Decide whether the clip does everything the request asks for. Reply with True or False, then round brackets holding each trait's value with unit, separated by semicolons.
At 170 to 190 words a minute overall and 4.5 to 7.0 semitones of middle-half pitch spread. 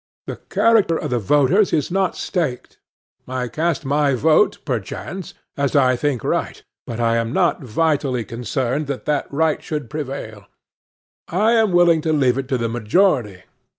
False (160 wpm; 4.8 semitones)